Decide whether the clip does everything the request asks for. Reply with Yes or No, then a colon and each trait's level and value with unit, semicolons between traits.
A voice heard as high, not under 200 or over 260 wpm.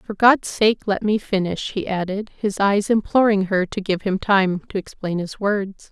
Yes: high, 200 Hz; fast, 205 wpm